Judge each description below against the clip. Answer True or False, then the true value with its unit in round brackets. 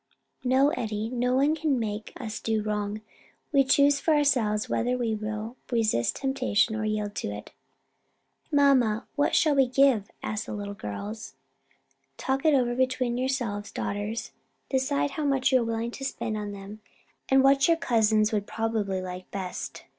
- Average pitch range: True (4.1 semitones)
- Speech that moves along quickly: False (165 wpm)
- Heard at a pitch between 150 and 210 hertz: False (230 Hz)